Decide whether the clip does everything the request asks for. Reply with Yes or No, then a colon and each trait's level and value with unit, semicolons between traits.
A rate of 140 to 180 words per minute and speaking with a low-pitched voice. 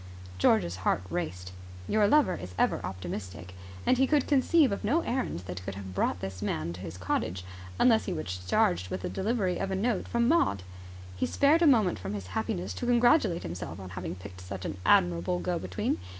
No: average, 200 wpm; very low, 95 Hz